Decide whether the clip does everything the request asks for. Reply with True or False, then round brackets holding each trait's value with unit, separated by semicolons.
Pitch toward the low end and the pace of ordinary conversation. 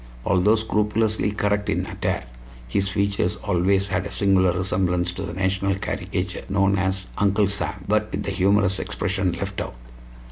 True (95 Hz; 155 wpm)